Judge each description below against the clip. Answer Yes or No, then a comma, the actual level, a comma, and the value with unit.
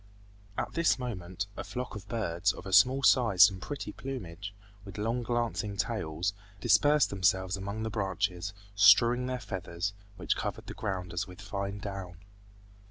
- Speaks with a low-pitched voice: Yes, low, 100 Hz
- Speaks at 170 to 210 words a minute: No, average, 160 wpm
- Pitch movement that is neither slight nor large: Yes, average, 3.9 semitones